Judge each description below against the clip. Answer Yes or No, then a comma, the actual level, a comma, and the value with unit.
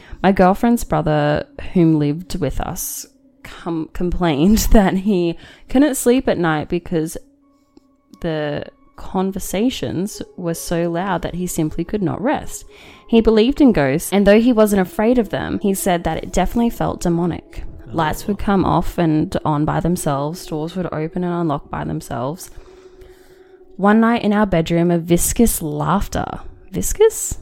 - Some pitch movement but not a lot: No, wide, 6.0 semitones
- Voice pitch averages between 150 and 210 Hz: Yes, medium, 185 Hz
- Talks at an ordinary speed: Yes, average, 150 wpm